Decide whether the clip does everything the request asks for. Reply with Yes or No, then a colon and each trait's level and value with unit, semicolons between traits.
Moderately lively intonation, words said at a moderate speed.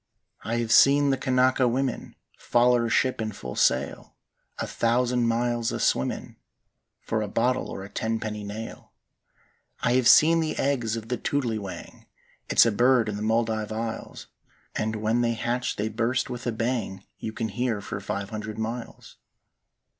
No: narrow, 2.3 semitones; average, 160 wpm